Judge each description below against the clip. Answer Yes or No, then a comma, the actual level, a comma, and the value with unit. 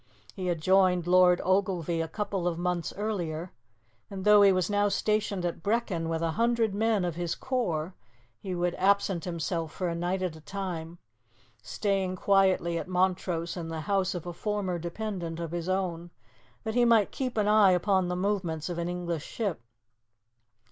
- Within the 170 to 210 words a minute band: Yes, average, 180 wpm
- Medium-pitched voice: Yes, medium, 180 Hz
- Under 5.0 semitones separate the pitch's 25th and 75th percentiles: Yes, average, 2.9 semitones